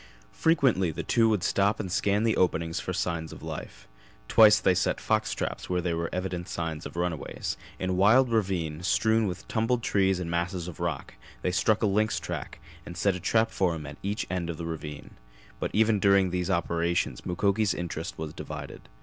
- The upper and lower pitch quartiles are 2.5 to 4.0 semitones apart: Yes, average, 3.6 semitones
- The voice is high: No, very low, 90 Hz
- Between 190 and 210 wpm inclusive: Yes, average, 200 wpm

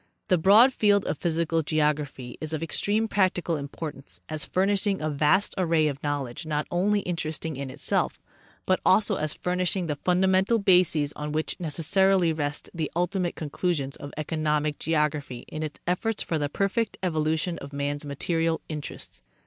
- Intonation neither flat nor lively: Yes, average, 3.8 semitones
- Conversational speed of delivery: Yes, average, 160 wpm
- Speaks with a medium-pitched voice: Yes, medium, 160 Hz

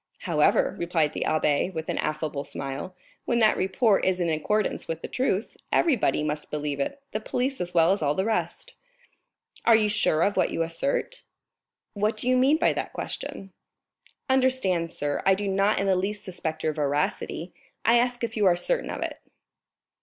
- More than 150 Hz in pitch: Yes, high, 190 Hz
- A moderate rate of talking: Yes, average, 185 wpm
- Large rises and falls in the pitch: Yes, wide, 6.1 semitones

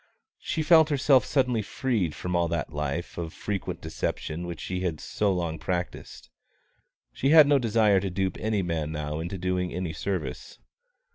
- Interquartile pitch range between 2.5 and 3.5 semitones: No, average, 4.7 semitones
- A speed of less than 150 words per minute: No, average, 165 wpm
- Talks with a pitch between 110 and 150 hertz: No, very low, 90 Hz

